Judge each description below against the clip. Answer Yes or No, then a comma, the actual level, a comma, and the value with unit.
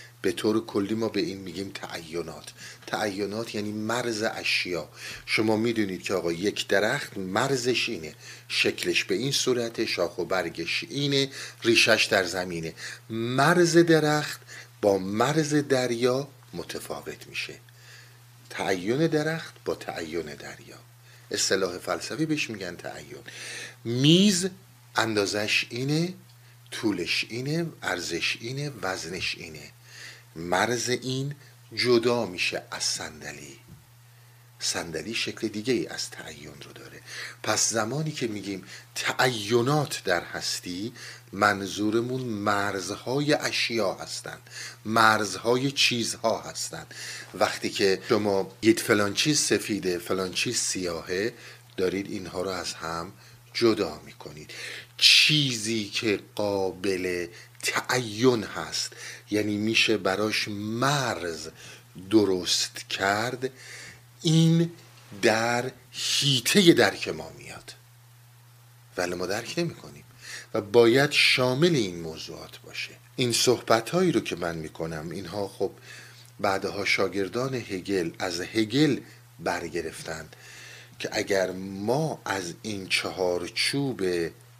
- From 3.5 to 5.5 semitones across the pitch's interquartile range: Yes, average, 3.8 semitones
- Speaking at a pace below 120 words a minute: Yes, slow, 105 wpm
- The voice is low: Yes, low, 120 Hz